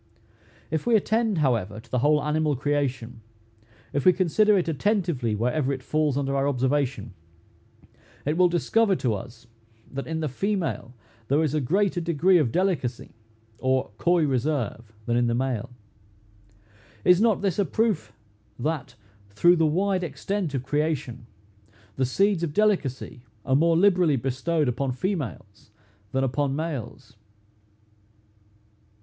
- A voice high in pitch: No, medium, 145 Hz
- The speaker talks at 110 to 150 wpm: Yes, average, 140 wpm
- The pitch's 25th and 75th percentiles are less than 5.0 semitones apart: No, wide, 5.5 semitones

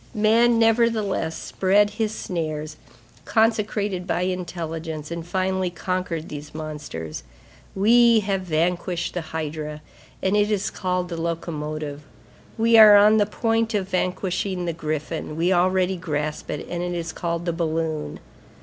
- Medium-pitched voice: Yes, medium, 180 Hz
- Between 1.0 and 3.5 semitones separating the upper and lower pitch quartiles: No, average, 4.3 semitones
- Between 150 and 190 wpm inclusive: No, average, 140 wpm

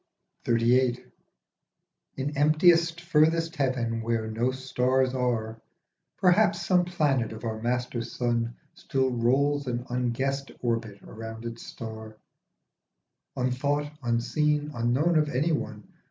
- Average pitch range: Yes, average, 4.0 semitones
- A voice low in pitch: Yes, low, 125 Hz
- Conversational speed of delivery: No, slow, 110 wpm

